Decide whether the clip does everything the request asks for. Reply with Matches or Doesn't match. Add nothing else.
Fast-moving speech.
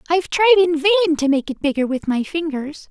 Matches